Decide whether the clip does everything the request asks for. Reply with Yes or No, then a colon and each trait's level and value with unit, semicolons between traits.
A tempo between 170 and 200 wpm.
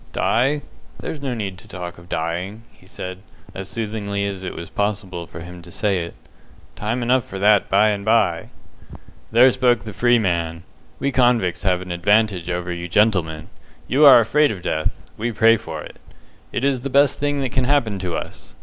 Yes: average, 195 wpm